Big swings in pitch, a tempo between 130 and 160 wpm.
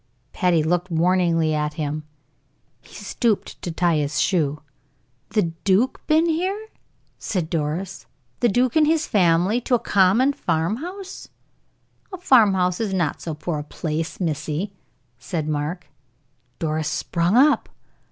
Yes: wide, 6.4 semitones; average, 140 wpm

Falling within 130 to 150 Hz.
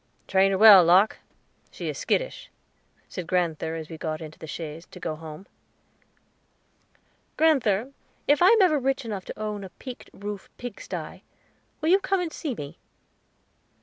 No: high, 200 Hz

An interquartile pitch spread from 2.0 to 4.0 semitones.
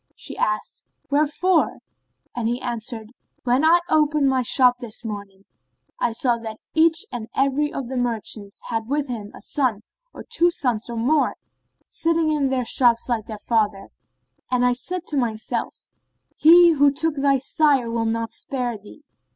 No: average, 4.5 semitones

